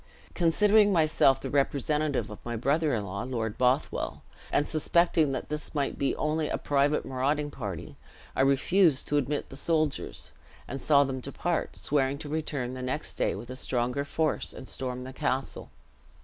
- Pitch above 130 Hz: Yes, medium, 140 Hz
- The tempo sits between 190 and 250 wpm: No, average, 165 wpm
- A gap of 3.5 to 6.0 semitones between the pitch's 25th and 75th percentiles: No, average, 3.0 semitones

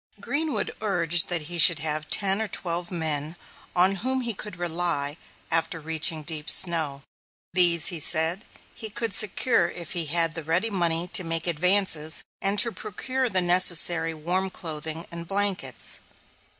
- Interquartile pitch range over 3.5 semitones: No, average, 3.2 semitones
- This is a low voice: No, medium, 175 Hz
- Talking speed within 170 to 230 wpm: No, average, 155 wpm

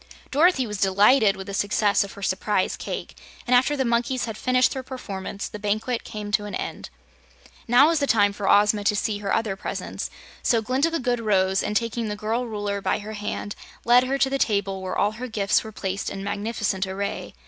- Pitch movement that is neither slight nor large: Yes, average, 3.4 semitones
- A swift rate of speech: Yes, fast, 215 wpm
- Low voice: No, high, 210 Hz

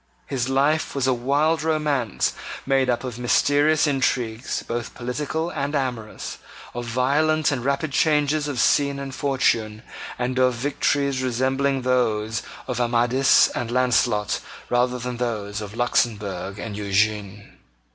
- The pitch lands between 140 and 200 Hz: No, low, 125 Hz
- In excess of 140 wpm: No, slow, 135 wpm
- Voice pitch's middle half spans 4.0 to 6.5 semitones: No, average, 3.1 semitones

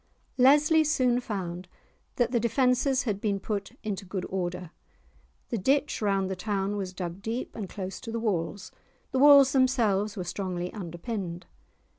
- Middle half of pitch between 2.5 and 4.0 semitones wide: No, average, 5.1 semitones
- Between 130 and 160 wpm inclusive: Yes, average, 155 wpm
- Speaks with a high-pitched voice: Yes, high, 205 Hz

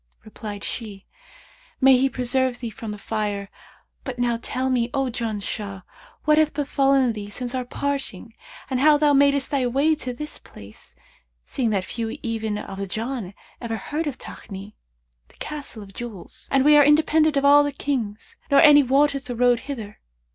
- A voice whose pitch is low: No, very high, 250 Hz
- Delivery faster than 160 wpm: Yes, average, 175 wpm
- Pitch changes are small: No, average, 4.5 semitones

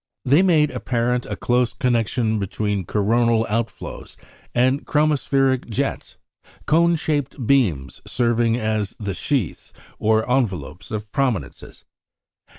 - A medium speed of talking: No, slow, 110 wpm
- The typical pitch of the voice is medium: No, low, 120 Hz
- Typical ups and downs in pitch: Yes, average, 3.9 semitones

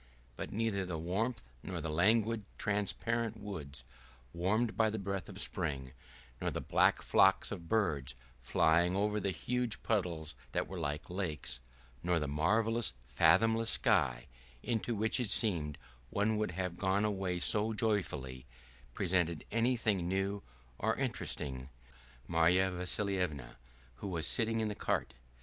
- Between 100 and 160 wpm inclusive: Yes, average, 140 wpm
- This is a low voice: Yes, very low, 95 Hz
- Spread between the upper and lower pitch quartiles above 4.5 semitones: Yes, average, 4.9 semitones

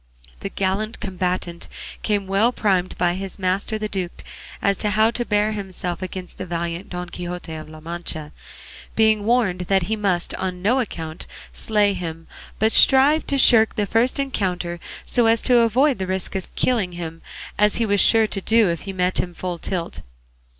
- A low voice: No, high, 195 Hz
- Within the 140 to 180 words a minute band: No, average, 190 wpm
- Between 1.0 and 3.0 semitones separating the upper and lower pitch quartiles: No, average, 3.5 semitones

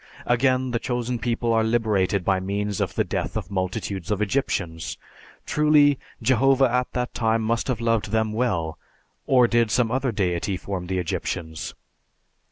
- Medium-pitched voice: No, low, 110 Hz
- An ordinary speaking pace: Yes, average, 160 wpm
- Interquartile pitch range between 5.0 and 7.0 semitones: No, average, 4.1 semitones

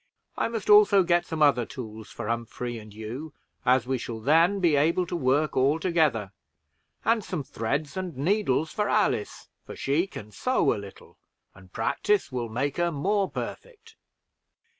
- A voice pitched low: No, medium, 150 Hz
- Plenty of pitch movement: Yes, wide, 7.4 semitones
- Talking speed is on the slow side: No, average, 165 wpm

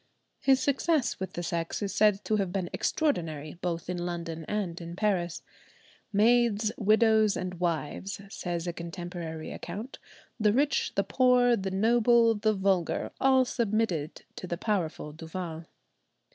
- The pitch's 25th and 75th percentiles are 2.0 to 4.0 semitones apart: No, average, 4.5 semitones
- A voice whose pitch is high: Yes, high, 195 Hz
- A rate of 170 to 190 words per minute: No, average, 145 wpm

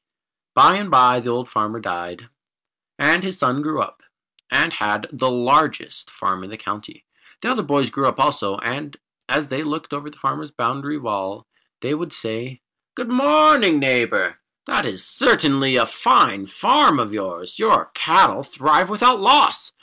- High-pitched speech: No, low, 135 Hz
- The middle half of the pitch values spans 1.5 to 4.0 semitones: No, wide, 5.5 semitones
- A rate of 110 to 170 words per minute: Yes, average, 165 wpm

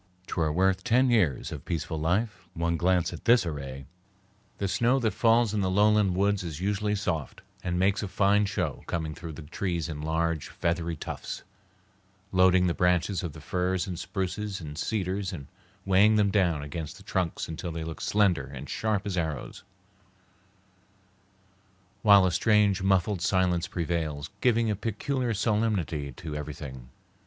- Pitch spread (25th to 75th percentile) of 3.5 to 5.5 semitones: Yes, average, 4.0 semitones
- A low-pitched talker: Yes, very low, 90 Hz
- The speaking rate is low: No, average, 165 wpm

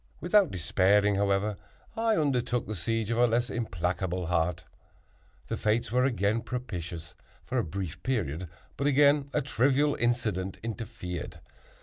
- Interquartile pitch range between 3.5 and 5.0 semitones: No, wide, 5.4 semitones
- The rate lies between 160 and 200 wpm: No, slow, 135 wpm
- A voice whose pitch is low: Yes, low, 110 Hz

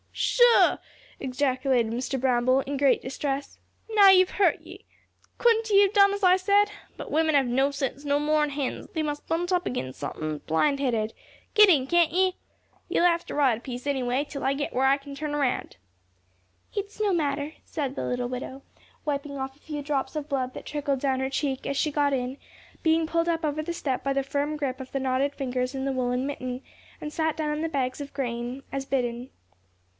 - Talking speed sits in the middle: No, fast, 210 wpm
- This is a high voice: Yes, very high, 280 Hz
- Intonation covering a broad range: No, average, 3.1 semitones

